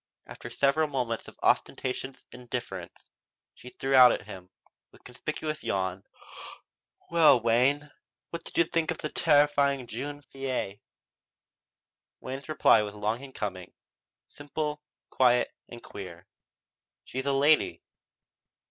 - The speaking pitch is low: Yes, low, 130 Hz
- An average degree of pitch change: Yes, average, 4.1 semitones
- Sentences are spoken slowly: Yes, slow, 125 wpm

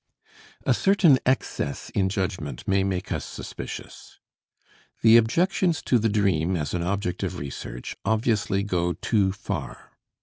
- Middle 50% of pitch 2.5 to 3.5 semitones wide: No, average, 4.1 semitones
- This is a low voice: Yes, low, 100 Hz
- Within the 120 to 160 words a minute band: Yes, slow, 135 wpm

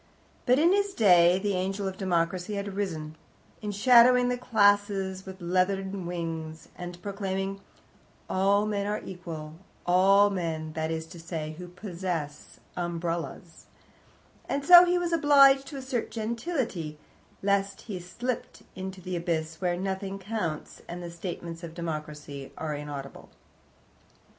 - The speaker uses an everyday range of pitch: Yes, average, 3.5 semitones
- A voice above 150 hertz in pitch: Yes, high, 190 Hz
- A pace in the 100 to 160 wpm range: Yes, slow, 135 wpm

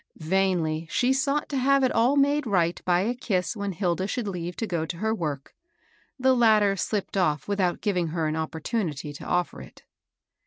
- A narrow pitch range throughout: No, wide, 5.5 semitones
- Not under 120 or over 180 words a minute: No, average, 190 wpm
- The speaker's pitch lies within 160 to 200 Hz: Yes, high, 190 Hz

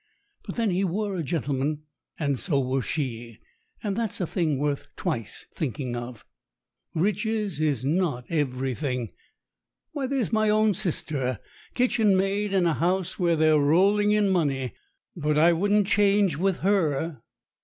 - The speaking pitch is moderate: Yes, medium, 170 Hz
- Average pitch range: No, wide, 6.3 semitones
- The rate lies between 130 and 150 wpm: Yes, average, 145 wpm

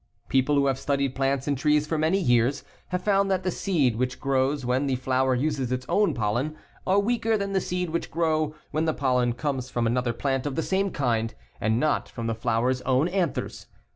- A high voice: No, medium, 140 Hz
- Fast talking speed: Yes, fast, 210 wpm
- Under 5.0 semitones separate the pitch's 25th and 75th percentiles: Yes, average, 4.4 semitones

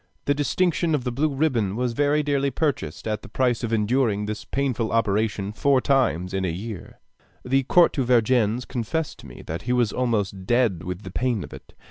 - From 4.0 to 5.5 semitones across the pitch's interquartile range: Yes, average, 4.6 semitones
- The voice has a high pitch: No, low, 120 Hz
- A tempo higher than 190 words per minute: Yes, average, 200 wpm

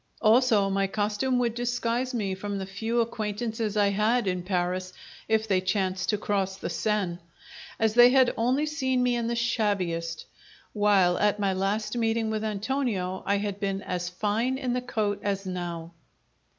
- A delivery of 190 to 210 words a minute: No, average, 170 wpm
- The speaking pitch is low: No, high, 210 Hz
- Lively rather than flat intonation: No, average, 3.5 semitones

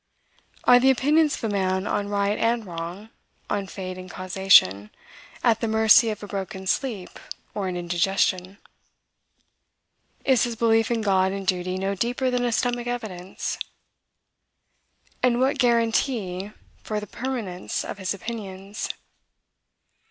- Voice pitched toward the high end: Yes, high, 205 Hz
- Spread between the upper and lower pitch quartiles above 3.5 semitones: Yes, average, 3.9 semitones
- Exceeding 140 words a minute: No, slow, 135 wpm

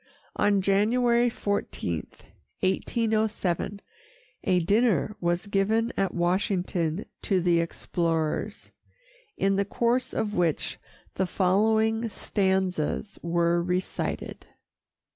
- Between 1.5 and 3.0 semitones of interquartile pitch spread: No, average, 3.8 semitones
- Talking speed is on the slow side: Yes, slow, 90 wpm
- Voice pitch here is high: Yes, high, 195 Hz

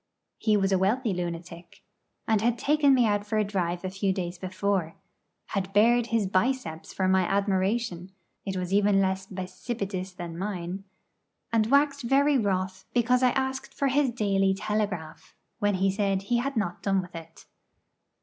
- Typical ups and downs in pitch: Yes, average, 3.8 semitones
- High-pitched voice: Yes, high, 195 Hz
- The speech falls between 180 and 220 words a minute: No, average, 170 wpm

